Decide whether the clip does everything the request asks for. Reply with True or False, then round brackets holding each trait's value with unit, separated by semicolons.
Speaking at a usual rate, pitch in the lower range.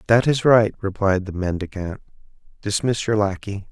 True (145 wpm; 105 Hz)